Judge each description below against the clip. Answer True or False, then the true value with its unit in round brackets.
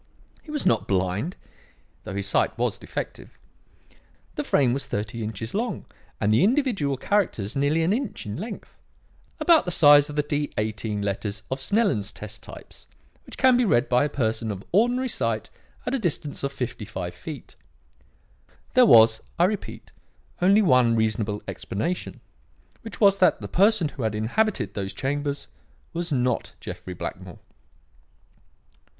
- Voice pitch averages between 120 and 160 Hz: True (140 Hz)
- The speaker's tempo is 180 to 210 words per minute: False (155 wpm)